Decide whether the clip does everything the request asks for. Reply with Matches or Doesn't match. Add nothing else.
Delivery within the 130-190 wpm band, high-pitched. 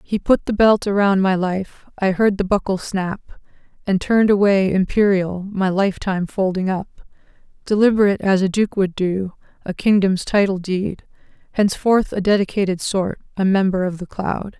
Matches